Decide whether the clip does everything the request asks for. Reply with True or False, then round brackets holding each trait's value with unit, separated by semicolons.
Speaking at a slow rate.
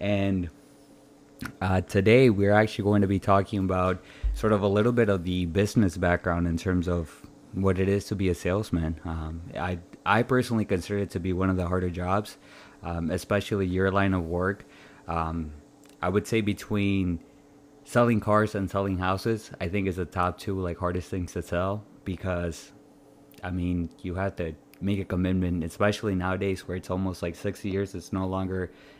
False (185 wpm)